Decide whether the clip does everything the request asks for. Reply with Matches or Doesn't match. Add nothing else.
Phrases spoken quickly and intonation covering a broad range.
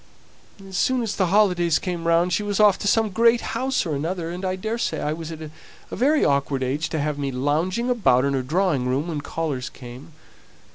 Matches